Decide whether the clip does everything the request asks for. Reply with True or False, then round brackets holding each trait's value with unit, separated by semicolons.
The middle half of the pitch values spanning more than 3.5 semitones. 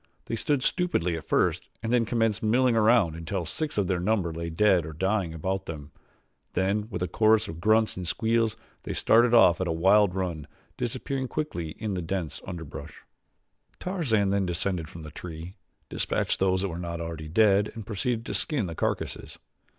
True (5.0 semitones)